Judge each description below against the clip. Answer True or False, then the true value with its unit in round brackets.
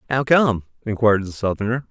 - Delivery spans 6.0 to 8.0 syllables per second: True (6.3 syllables/s)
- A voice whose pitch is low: True (115 Hz)